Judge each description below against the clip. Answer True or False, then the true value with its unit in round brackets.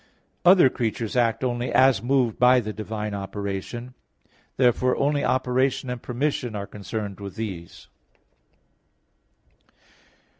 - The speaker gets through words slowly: True (110 wpm)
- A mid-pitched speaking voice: False (120 Hz)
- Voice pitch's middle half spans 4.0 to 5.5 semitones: False (3.4 semitones)